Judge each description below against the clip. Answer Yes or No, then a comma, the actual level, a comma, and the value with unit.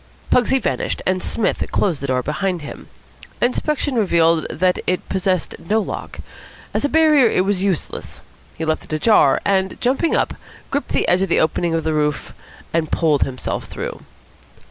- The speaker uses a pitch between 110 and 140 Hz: No, medium, 185 Hz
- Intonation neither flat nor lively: No, wide, 5.8 semitones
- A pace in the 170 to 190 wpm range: Yes, average, 180 wpm